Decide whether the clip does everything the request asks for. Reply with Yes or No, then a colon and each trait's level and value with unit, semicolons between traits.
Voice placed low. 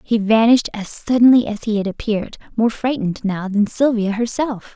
No: high, 220 Hz